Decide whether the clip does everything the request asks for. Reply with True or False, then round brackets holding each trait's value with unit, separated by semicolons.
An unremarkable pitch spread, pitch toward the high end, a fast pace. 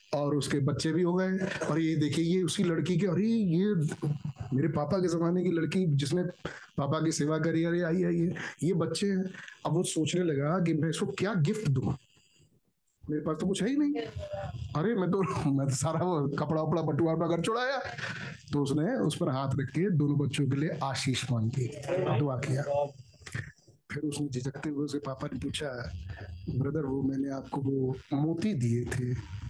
False (4.0 semitones; 155 Hz; 195 wpm)